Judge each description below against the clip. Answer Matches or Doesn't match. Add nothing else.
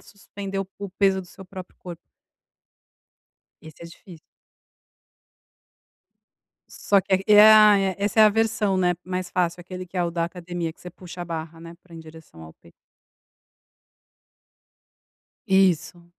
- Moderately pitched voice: Matches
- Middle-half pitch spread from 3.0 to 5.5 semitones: Doesn't match